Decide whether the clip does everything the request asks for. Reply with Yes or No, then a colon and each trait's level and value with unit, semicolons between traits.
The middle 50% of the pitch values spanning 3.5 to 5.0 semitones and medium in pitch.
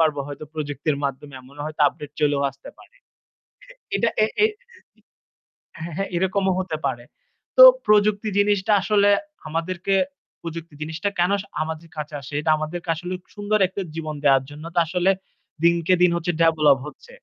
Yes: average, 4.0 semitones; medium, 165 Hz